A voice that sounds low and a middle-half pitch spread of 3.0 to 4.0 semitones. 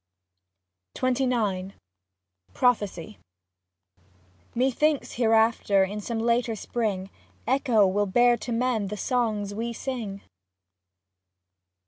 No: high, 225 Hz; average, 3.3 semitones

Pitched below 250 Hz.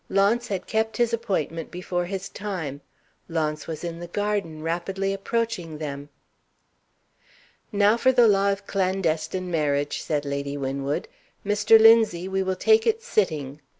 Yes: medium, 185 Hz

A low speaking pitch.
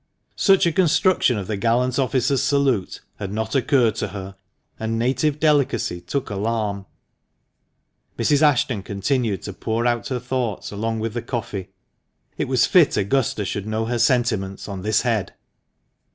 Yes: low, 115 Hz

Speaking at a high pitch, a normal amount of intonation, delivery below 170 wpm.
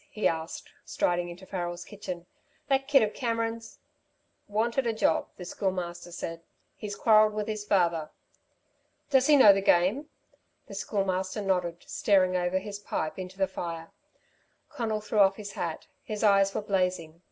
Yes: high, 195 Hz; average, 3.4 semitones; average, 160 wpm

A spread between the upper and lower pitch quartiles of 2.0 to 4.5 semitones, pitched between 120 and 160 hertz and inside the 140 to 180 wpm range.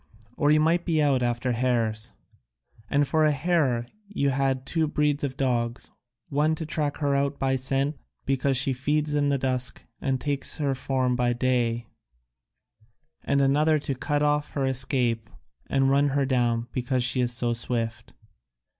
Yes: average, 2.7 semitones; low, 135 Hz; average, 170 wpm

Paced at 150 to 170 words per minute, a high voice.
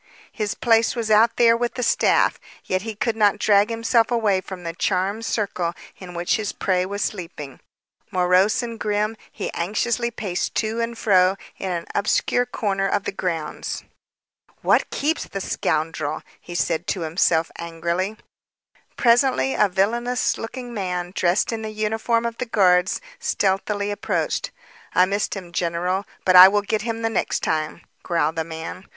Yes: average, 165 wpm; high, 200 Hz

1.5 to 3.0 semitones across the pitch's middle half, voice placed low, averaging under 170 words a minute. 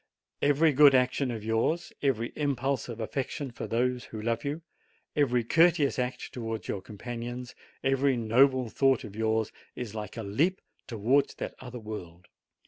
No: average, 3.6 semitones; low, 125 Hz; average, 155 wpm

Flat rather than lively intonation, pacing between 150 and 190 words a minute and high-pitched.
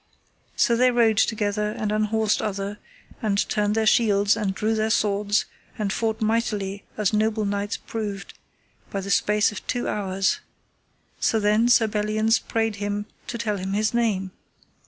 Yes: narrow, 1.5 semitones; average, 155 wpm; high, 210 Hz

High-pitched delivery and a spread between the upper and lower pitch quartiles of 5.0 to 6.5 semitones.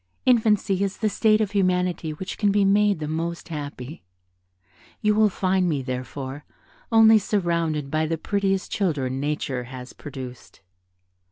No: medium, 175 Hz; wide, 5.6 semitones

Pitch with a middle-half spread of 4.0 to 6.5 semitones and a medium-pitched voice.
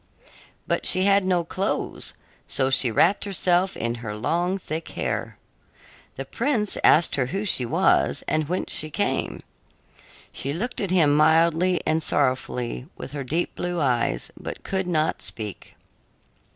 Yes: wide, 5.6 semitones; medium, 160 Hz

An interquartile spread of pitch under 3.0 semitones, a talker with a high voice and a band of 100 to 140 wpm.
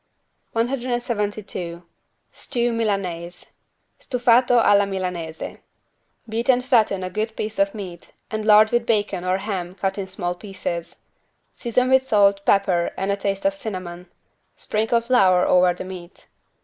No: average, 4.1 semitones; high, 200 Hz; slow, 135 wpm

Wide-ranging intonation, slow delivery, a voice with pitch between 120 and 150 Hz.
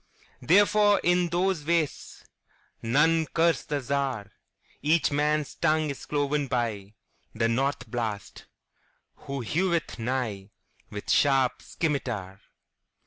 Yes: wide, 5.9 semitones; slow, 85 wpm; medium, 140 Hz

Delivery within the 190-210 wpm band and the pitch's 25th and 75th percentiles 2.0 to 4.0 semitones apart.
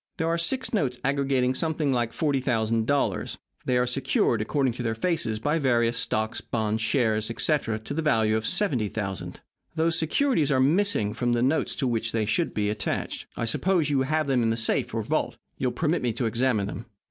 No: average, 195 wpm; average, 5.1 semitones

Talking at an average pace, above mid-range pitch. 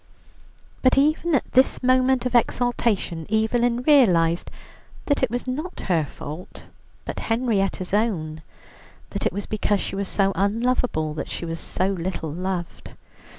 Yes: average, 145 wpm; high, 210 Hz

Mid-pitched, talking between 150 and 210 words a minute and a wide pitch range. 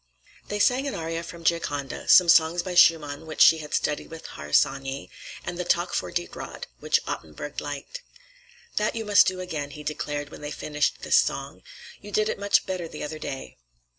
No: medium, 165 Hz; average, 195 wpm; average, 3.7 semitones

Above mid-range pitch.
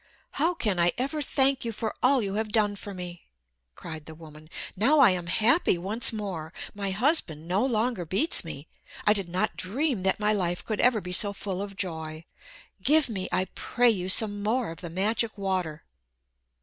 Yes: high, 200 Hz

